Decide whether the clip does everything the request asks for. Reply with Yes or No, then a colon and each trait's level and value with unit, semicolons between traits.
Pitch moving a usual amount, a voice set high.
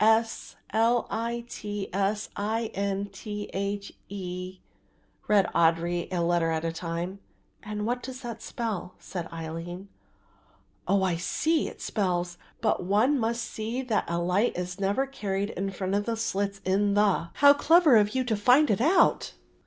Yes: average, 3.9 semitones; high, 200 Hz